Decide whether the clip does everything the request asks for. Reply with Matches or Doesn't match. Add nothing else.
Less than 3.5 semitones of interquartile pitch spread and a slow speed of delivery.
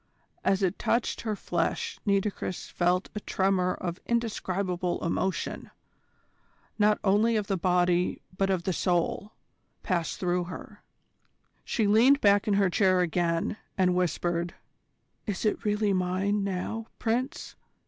Matches